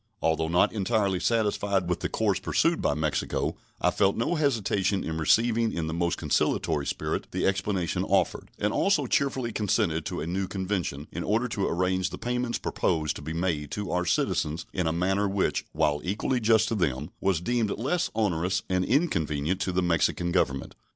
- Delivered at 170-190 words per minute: Yes, average, 185 wpm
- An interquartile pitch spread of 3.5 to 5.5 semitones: Yes, average, 4.7 semitones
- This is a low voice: Yes, very low, 95 Hz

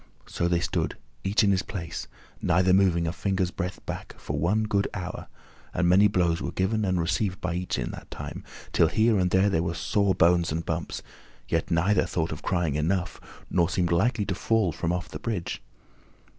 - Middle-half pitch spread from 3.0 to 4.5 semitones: No, narrow, 2.4 semitones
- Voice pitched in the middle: No, very low, 90 Hz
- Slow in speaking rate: No, average, 195 wpm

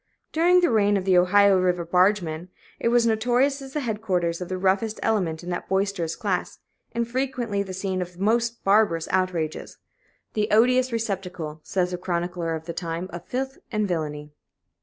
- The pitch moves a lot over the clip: No, average, 4.3 semitones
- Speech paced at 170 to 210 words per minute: Yes, average, 175 wpm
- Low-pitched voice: No, high, 190 Hz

